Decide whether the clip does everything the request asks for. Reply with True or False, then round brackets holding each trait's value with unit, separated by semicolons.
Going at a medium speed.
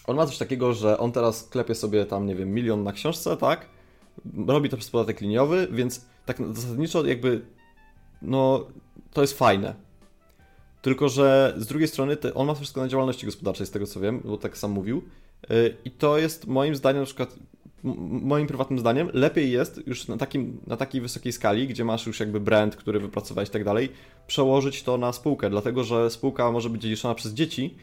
False (190 wpm)